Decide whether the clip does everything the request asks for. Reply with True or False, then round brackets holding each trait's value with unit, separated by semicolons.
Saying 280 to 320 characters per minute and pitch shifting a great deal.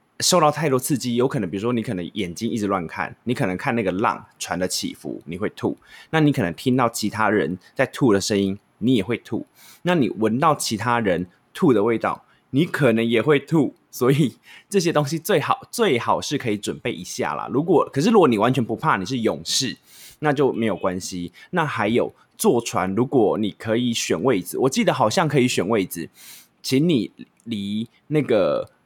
True (285 characters per minute; 6.1 semitones)